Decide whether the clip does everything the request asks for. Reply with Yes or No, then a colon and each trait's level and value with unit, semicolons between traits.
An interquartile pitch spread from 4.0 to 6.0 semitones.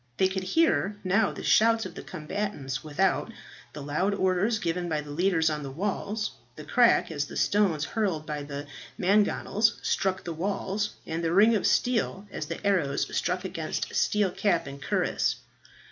Yes: average, 4.9 semitones